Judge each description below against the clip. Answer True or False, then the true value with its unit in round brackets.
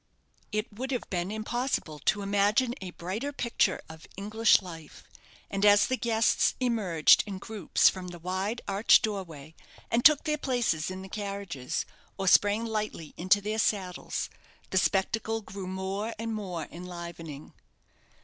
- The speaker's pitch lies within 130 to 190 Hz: False (200 Hz)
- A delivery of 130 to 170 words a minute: True (150 wpm)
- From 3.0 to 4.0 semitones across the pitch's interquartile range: True (3.6 semitones)